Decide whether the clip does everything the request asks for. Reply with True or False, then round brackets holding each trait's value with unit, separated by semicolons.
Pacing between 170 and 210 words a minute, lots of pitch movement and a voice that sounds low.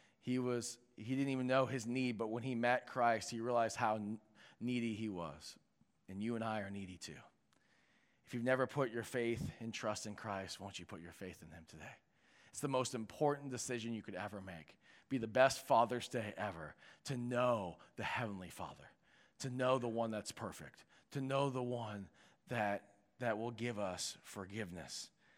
False (190 wpm; 3.4 semitones; 115 Hz)